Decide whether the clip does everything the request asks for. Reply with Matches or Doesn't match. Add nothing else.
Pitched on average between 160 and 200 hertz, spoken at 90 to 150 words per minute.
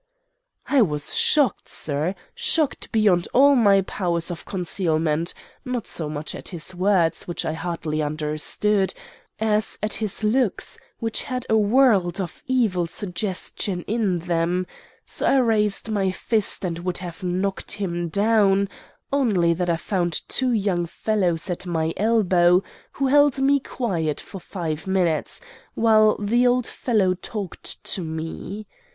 Matches